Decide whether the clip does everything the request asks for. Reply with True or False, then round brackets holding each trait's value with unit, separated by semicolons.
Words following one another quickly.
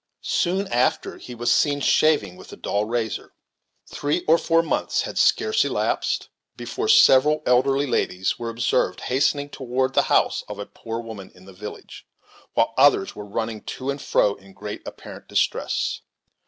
False (165 wpm)